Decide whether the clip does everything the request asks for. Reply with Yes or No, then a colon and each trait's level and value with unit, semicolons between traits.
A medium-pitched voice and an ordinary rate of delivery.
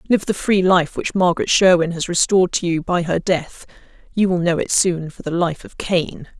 No: medium, 175 Hz; fast, 215 wpm